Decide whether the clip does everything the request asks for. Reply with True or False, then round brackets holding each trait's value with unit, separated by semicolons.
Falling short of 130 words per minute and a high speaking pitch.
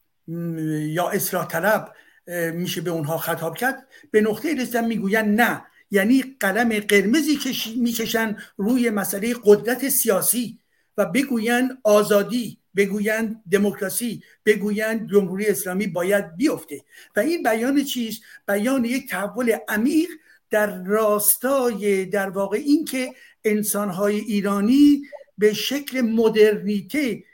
True (110 wpm; 215 Hz)